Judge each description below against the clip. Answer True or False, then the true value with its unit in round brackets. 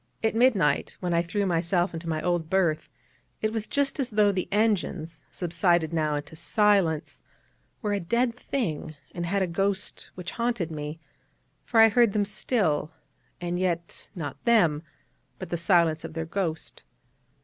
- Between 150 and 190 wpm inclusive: True (160 wpm)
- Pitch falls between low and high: True (180 Hz)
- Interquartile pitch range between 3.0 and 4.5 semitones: True (4.1 semitones)